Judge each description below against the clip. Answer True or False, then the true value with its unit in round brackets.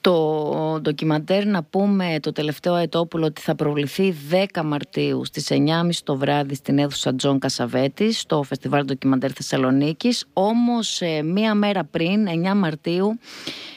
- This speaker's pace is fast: False (130 wpm)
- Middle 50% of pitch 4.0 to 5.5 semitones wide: True (5.1 semitones)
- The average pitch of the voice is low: False (160 Hz)